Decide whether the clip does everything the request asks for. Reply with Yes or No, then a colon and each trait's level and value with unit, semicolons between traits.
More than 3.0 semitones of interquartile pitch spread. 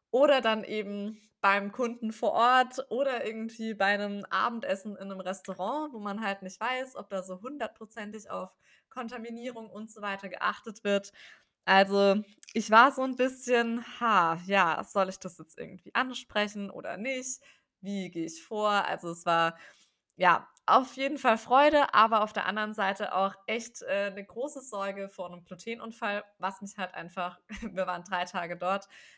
Yes: average, 3.4 semitones